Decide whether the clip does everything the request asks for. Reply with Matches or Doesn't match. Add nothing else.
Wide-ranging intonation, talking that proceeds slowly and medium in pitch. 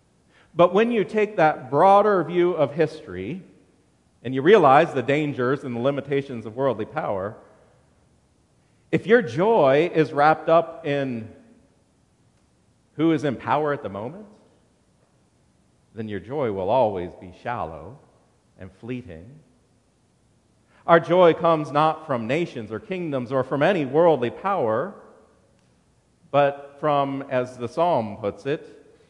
Doesn't match